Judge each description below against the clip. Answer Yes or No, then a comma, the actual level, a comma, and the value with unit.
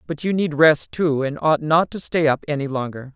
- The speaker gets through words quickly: Yes, fast, 250 wpm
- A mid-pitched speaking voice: Yes, medium, 150 Hz